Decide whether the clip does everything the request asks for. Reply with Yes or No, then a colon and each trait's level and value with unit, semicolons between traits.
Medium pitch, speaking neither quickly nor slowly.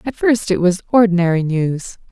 No: high, 195 Hz; average, 170 wpm